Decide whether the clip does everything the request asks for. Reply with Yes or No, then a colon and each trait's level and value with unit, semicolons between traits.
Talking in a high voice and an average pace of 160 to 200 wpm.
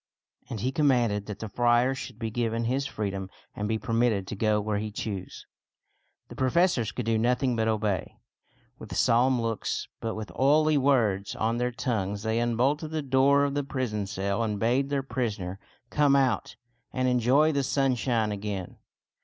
No: low, 115 Hz; average, 170 wpm